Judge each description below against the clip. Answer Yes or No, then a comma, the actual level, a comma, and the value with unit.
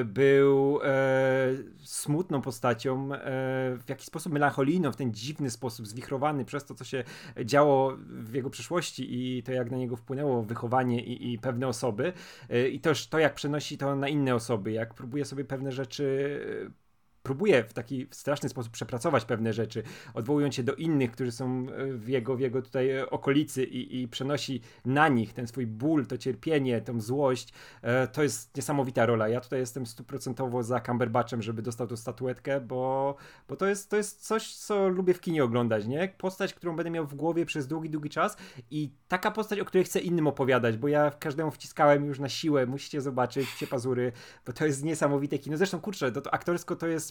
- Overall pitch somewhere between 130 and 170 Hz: Yes, low, 135 Hz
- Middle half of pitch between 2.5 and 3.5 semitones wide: Yes, average, 2.9 semitones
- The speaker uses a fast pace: Yes, fast, 190 wpm